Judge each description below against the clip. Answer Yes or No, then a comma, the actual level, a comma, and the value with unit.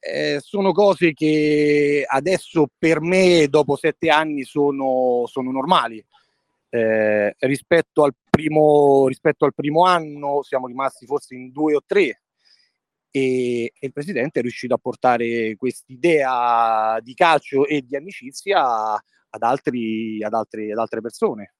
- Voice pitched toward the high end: No, medium, 140 Hz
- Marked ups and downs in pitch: No, average, 4.1 semitones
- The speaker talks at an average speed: Yes, average, 135 wpm